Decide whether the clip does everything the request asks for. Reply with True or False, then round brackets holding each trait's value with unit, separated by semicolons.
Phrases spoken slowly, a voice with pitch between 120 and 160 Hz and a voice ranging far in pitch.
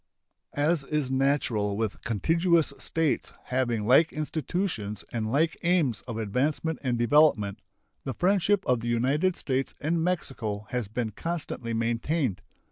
True (130 wpm; 135 Hz; 5.9 semitones)